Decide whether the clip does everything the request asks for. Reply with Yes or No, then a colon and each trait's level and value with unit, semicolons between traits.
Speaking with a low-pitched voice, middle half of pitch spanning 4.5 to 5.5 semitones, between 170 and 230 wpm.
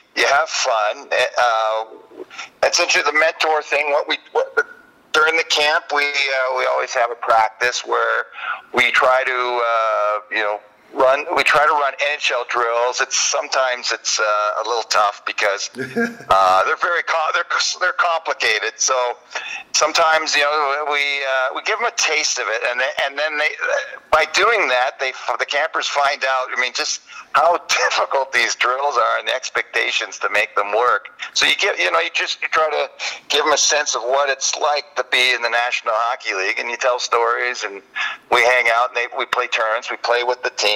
Yes: low, 130 Hz; average, 4.8 semitones; average, 200 wpm